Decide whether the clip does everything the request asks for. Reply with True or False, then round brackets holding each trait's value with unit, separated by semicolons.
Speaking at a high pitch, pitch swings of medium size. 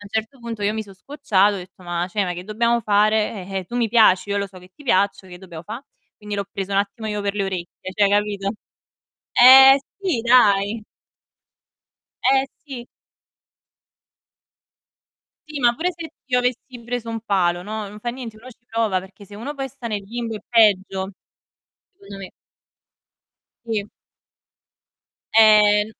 True (210 Hz; 3.3 semitones)